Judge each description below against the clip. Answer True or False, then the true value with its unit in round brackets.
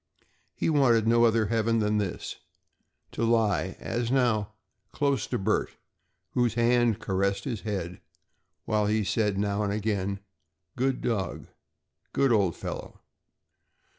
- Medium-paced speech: False (130 wpm)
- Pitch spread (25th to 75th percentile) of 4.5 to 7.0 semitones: False (2.7 semitones)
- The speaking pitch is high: False (110 Hz)